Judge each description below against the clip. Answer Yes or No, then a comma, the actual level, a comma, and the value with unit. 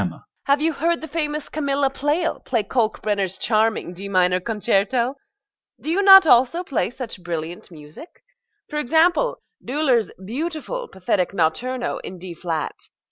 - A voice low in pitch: No, high, 245 Hz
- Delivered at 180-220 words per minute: No, average, 150 wpm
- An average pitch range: No, wide, 8.2 semitones